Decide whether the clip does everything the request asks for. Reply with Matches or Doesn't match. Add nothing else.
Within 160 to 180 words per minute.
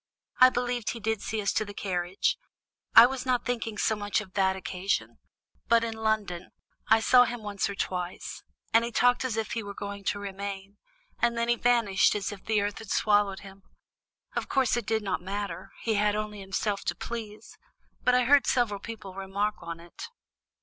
Doesn't match